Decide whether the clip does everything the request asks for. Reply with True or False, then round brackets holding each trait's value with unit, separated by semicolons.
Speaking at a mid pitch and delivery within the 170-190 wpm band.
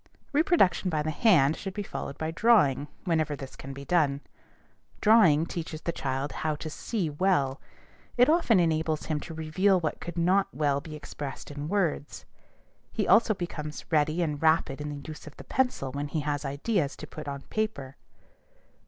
True (155 Hz; 180 wpm)